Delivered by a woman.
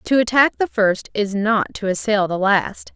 Yes: female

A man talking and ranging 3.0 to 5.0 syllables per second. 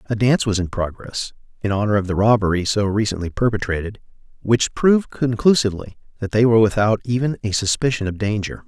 No: male; 6.2 syllables/s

